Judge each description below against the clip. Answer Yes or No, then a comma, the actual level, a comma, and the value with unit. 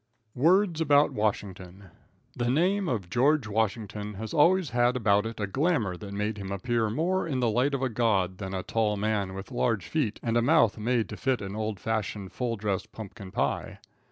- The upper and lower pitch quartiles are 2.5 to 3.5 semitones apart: No, average, 4.0 semitones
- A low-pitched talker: Yes, low, 110 Hz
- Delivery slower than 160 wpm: No, average, 195 wpm